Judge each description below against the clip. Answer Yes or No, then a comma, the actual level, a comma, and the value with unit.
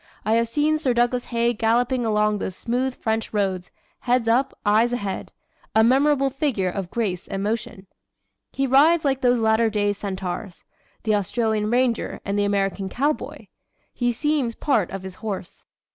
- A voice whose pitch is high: Yes, high, 230 Hz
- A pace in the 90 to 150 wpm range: No, average, 160 wpm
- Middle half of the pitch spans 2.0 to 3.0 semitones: No, average, 3.6 semitones